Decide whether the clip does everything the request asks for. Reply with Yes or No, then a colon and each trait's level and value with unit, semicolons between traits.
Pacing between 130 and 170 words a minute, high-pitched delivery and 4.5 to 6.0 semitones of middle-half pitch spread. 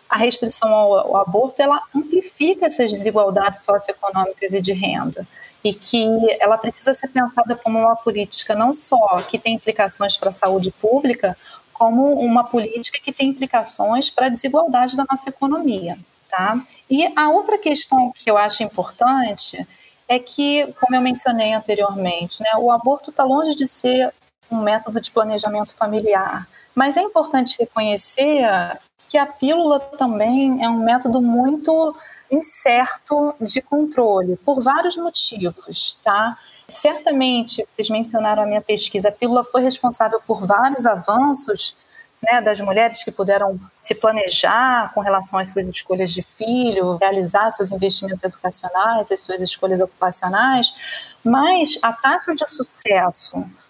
Yes: average, 145 wpm; high, 230 Hz; average, 4.8 semitones